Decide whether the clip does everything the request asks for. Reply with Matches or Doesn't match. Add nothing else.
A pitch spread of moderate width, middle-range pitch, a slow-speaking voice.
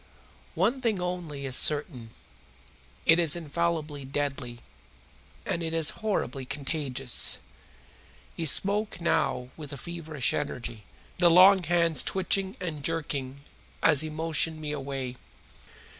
Matches